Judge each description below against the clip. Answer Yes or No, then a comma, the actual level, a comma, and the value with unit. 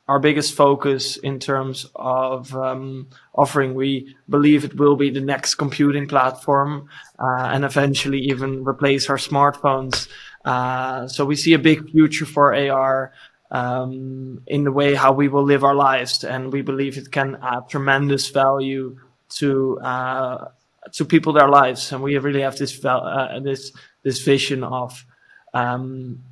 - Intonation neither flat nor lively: No, narrow, 1.4 semitones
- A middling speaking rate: Yes, average, 155 wpm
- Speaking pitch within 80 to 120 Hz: No, low, 135 Hz